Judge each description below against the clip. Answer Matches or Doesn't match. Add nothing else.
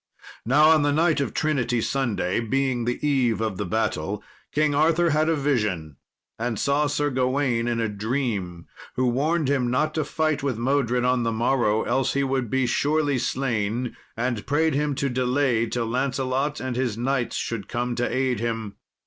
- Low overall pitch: Matches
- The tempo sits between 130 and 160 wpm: Doesn't match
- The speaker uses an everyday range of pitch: Matches